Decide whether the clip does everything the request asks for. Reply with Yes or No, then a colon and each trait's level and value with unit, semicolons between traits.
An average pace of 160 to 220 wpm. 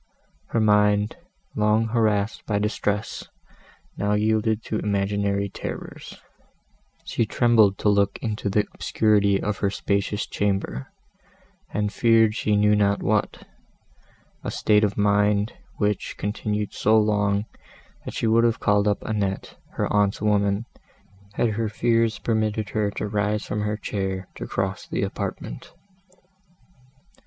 No: slow, 135 wpm